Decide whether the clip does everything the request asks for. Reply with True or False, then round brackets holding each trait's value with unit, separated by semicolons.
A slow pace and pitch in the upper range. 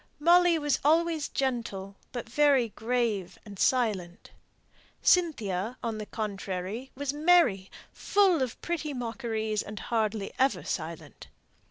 True (120 wpm; 235 Hz)